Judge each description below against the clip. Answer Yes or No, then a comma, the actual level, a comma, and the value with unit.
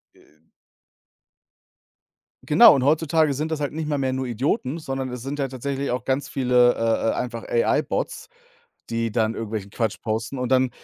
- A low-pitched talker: Yes, low, 130 Hz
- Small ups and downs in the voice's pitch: No, average, 3.3 semitones